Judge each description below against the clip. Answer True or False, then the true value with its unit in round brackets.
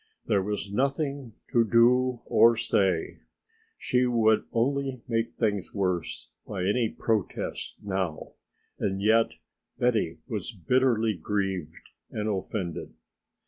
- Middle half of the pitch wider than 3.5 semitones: True (3.9 semitones)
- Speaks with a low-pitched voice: True (110 Hz)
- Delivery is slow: True (110 wpm)